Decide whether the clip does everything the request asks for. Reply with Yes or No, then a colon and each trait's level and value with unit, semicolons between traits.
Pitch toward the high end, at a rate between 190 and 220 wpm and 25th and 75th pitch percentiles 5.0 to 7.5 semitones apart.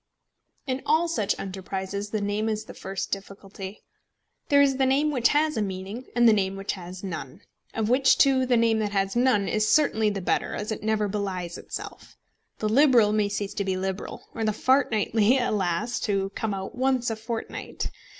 No: high, 215 Hz; average, 195 wpm; average, 4.0 semitones